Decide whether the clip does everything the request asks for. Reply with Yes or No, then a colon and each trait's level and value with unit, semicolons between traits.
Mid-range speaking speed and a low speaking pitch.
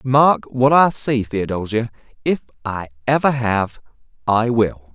Yes: average, 145 wpm; low, 115 Hz